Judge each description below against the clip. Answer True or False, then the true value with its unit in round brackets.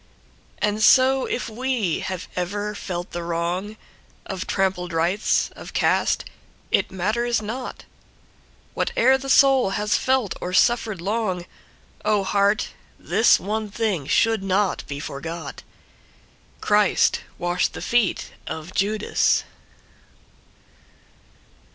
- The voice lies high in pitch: True (205 Hz)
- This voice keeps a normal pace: False (100 wpm)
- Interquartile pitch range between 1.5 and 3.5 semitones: False (4.1 semitones)